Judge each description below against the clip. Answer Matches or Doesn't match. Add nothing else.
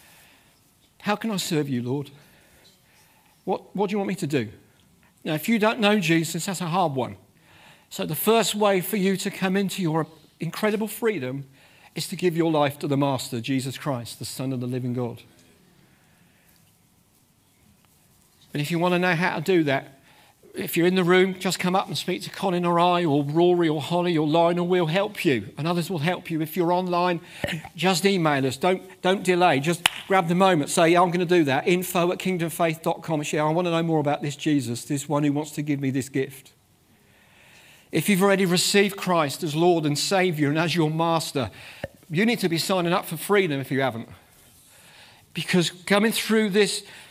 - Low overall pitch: Doesn't match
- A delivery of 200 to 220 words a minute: Matches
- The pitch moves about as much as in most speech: Matches